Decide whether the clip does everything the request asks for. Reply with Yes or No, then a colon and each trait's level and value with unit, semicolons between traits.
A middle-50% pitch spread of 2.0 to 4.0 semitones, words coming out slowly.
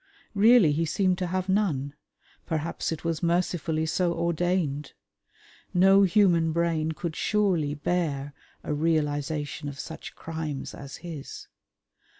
Yes: average, 3.2 semitones; slow, 125 wpm